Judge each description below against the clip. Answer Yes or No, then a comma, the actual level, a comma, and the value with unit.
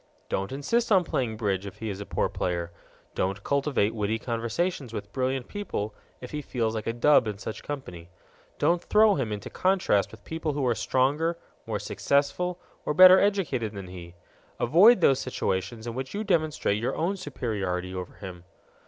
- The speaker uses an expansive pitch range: Yes, wide, 7.5 semitones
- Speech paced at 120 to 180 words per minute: Yes, average, 175 wpm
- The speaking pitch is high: No, low, 125 Hz